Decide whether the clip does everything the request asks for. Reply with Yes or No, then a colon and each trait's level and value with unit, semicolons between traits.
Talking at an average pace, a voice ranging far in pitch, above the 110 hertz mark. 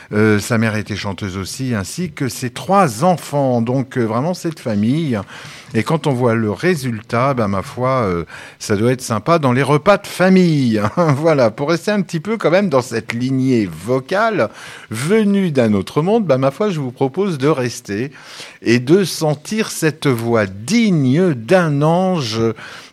Yes: average, 180 wpm; wide, 6.7 semitones; low, 135 Hz